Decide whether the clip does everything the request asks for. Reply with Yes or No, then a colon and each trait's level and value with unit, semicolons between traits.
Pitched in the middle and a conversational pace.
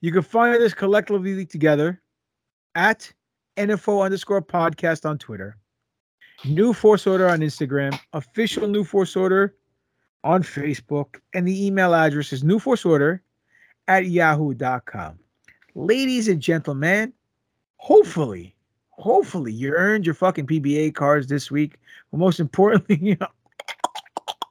No: medium, 170 Hz; slow, 120 wpm